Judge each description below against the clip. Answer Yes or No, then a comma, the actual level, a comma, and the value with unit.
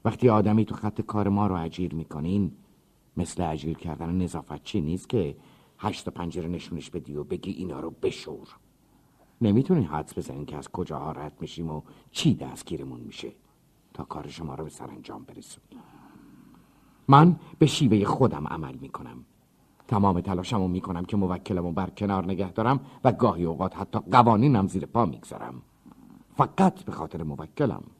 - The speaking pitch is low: Yes, very low, 90 Hz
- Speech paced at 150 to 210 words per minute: Yes, fast, 155 wpm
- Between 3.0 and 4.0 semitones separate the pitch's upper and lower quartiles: No, average, 4.9 semitones